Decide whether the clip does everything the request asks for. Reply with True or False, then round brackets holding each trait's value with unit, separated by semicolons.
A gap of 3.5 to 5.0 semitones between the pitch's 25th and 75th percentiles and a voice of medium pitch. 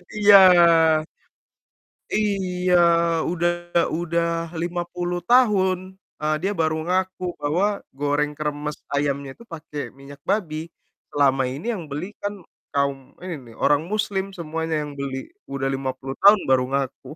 True (4.7 semitones; 160 Hz)